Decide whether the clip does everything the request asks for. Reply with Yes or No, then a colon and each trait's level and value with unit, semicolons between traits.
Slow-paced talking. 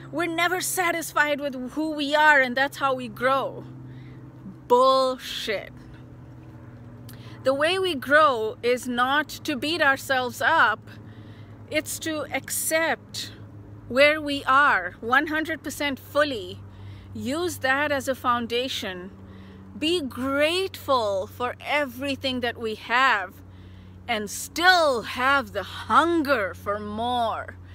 Yes: slow, 110 wpm